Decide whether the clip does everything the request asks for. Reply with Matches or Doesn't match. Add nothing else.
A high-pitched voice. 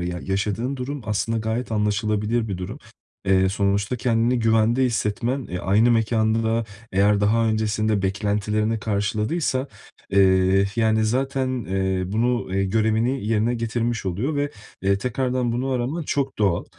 Doesn't match